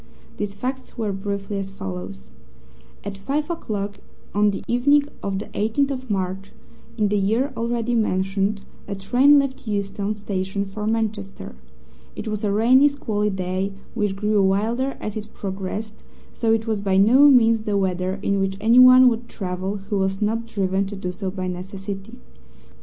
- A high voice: Yes, high, 205 Hz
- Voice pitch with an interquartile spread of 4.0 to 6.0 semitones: No, average, 2.8 semitones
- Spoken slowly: No, average, 165 wpm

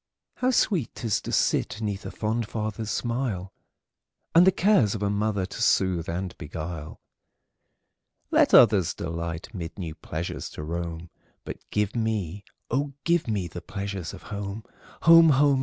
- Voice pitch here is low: Yes, low, 105 Hz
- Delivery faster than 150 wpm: No, average, 140 wpm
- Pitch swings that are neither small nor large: Yes, average, 5.0 semitones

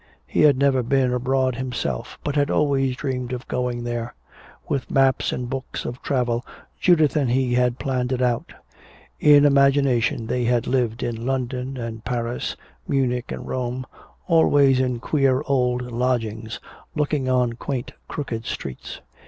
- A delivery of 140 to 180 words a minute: Yes, average, 150 wpm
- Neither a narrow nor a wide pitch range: No, narrow, 2.0 semitones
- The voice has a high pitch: No, low, 125 Hz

